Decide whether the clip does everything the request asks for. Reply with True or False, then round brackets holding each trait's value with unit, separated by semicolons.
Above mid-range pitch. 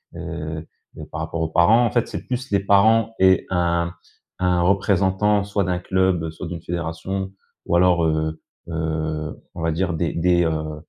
False (90 Hz)